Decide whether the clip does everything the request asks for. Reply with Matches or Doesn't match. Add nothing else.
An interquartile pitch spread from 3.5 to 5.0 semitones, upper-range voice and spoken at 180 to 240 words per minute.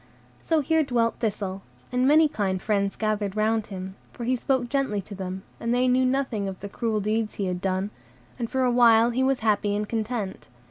Matches